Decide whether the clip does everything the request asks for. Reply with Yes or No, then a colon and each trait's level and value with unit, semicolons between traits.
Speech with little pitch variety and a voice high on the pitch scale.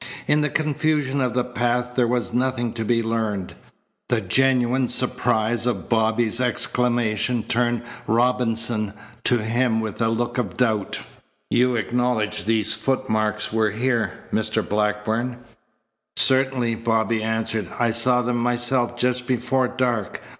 No: narrow, 2.0 semitones; low, 120 Hz